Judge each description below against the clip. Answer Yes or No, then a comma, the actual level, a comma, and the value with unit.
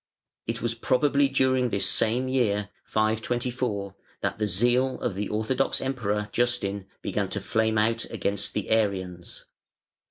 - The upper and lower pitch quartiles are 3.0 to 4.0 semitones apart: Yes, average, 3.5 semitones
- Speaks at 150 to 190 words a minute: No, slow, 135 wpm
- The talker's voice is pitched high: No, low, 110 Hz